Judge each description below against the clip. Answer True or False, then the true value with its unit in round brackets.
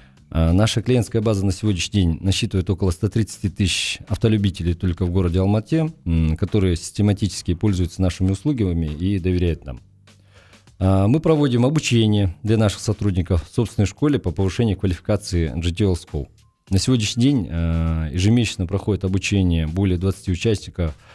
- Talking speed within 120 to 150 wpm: True (130 wpm)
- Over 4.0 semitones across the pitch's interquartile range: False (3.2 semitones)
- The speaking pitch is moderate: False (100 Hz)